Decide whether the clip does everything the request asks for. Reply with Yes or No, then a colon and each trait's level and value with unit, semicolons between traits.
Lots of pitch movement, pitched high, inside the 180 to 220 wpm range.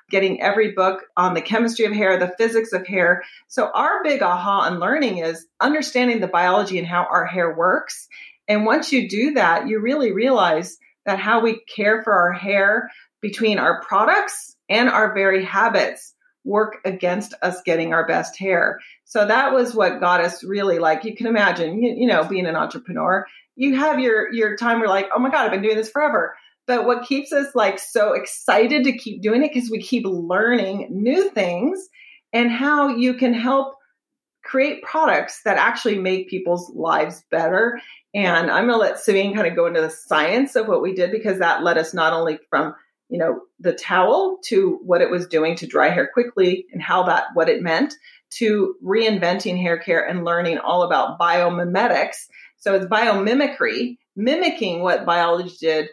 Yes: wide, 6.0 semitones; high, 215 Hz; average, 190 wpm